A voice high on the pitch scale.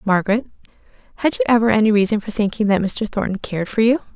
Yes: high, 210 Hz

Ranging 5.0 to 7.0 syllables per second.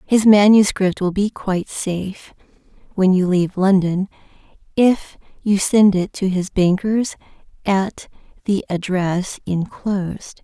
No: 3.6 syllables/s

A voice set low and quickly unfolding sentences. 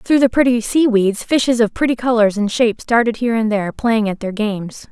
No: high, 225 Hz; fast, 230 wpm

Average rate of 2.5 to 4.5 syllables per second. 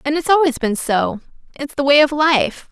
No: 5.0 syllables/s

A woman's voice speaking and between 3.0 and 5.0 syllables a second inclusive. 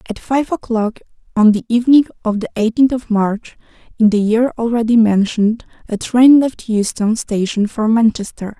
Yes: female; 4.9 syllables/s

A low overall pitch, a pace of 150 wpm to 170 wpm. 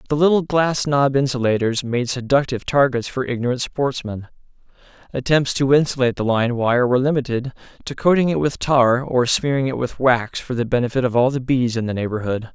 No: low, 130 Hz; average, 185 wpm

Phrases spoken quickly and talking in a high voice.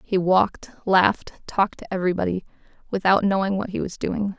No: average, 165 wpm; high, 195 Hz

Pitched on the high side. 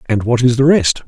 No: low, 125 Hz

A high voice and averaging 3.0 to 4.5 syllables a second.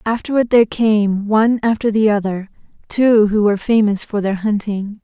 No: high, 215 Hz; 5.1 syllables/s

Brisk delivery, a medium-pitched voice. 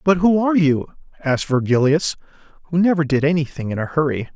No: average, 180 wpm; medium, 155 Hz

